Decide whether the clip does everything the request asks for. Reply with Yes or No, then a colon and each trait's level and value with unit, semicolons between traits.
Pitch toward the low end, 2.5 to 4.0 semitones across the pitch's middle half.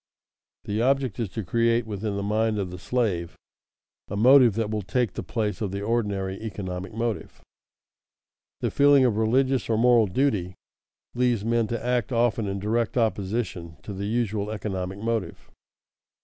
Yes: low, 110 Hz; average, 3.0 semitones